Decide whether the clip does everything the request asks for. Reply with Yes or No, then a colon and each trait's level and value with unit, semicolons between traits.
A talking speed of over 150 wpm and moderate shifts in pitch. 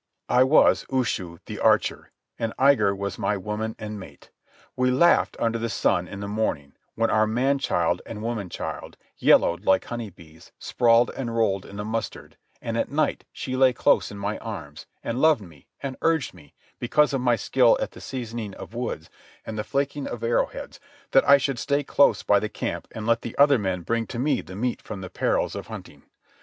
Yes: fast, 205 wpm; average, 4.2 semitones